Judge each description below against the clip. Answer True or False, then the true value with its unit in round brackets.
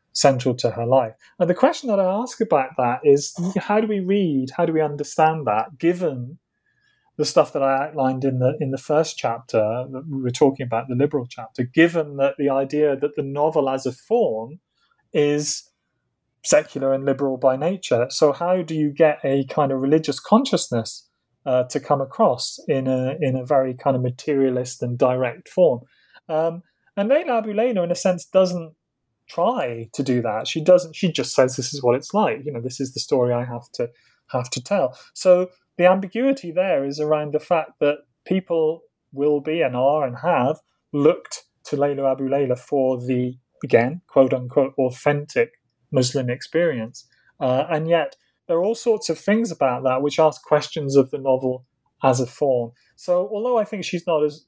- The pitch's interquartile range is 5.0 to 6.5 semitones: False (4.6 semitones)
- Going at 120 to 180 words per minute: False (190 wpm)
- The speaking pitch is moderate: True (145 Hz)